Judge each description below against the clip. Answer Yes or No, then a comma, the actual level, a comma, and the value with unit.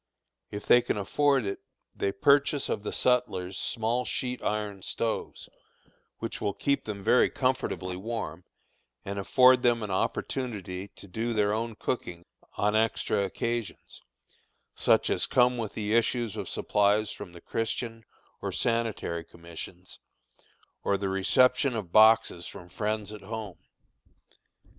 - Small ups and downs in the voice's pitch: No, average, 3.4 semitones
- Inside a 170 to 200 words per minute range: No, average, 140 wpm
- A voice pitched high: No, low, 110 Hz